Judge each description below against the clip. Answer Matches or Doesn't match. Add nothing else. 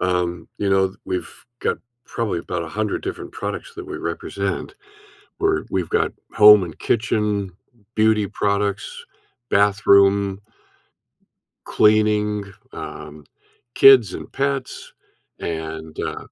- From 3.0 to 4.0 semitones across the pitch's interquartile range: Matches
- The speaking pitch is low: Matches